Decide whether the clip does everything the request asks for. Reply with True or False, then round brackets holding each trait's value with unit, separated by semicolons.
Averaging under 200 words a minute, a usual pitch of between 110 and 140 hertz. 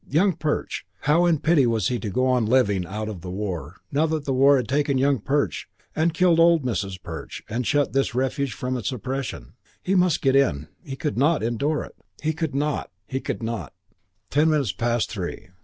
False (205 wpm; 135 Hz)